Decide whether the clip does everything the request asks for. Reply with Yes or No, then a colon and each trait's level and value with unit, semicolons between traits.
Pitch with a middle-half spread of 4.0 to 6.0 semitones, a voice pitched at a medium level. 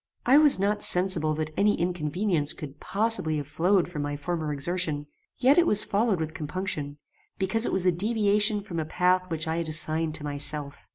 Yes: average, 4.6 semitones; medium, 175 Hz